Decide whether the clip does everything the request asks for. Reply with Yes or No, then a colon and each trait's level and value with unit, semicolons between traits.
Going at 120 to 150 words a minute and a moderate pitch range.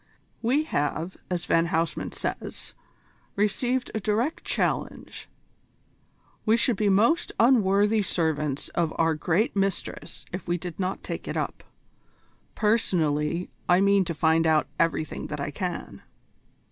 Yes: slow, 135 wpm; average, 4.7 semitones